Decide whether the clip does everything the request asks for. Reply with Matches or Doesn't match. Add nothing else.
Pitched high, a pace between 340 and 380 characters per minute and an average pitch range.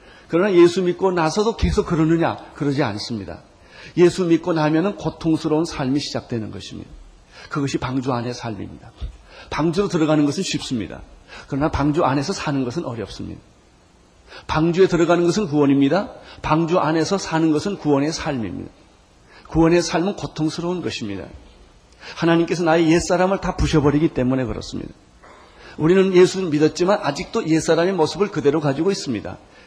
Doesn't match